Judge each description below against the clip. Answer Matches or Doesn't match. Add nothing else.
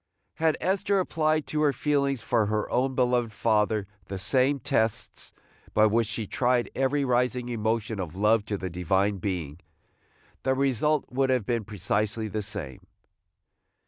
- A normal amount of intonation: Matches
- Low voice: Matches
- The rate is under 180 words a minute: Matches